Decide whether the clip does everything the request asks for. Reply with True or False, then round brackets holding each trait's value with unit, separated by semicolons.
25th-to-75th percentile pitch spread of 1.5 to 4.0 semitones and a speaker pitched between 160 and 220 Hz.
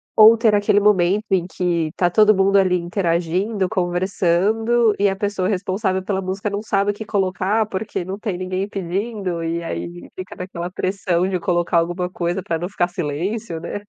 True (2.6 semitones; 190 Hz)